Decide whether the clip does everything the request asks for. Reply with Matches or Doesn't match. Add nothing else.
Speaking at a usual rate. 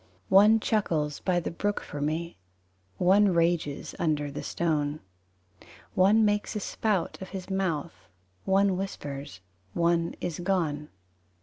Doesn't match